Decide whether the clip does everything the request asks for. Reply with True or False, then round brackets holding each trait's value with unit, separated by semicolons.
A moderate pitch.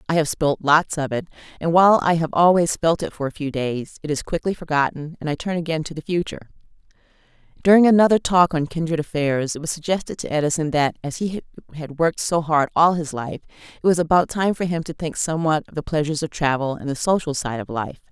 True (160 Hz)